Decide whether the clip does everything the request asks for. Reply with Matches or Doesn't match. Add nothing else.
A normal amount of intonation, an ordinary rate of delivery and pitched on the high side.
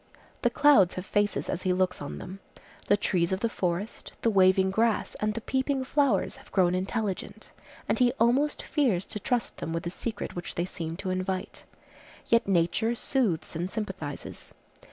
Matches